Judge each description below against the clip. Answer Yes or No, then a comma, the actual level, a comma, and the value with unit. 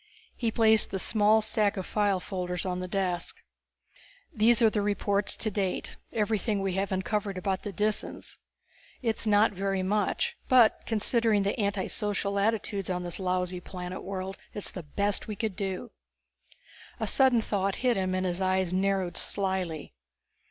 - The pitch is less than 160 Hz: No, high, 200 Hz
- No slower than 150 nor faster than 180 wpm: Yes, average, 160 wpm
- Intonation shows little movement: Yes, narrow, 2.3 semitones